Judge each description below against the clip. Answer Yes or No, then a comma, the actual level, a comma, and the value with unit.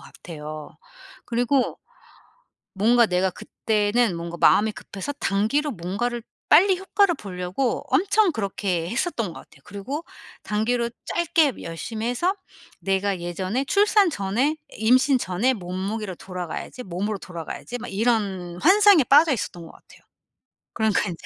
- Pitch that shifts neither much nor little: No, wide, 6.4 semitones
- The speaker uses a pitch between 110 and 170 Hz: No, high, 220 Hz